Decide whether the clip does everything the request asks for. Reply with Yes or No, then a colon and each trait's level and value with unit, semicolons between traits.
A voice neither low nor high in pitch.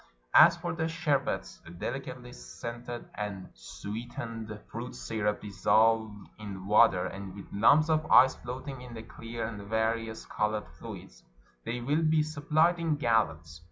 No: low, 115 Hz